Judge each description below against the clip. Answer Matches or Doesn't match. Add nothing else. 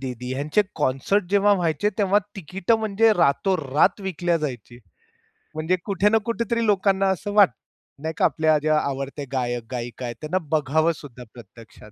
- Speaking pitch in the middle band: Matches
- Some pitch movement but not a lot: Doesn't match